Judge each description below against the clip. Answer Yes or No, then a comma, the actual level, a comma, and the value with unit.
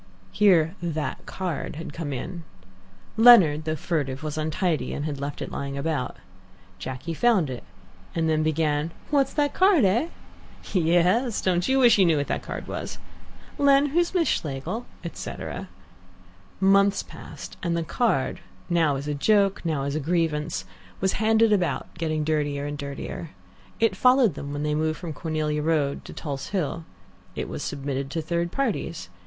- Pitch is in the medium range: Yes, medium, 165 Hz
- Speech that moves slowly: No, average, 160 wpm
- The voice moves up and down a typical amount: Yes, average, 5.0 semitones